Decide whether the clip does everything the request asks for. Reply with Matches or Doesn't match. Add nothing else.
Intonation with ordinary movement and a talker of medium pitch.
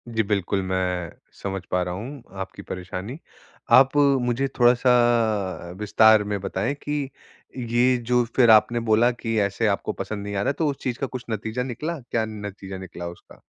Doesn't match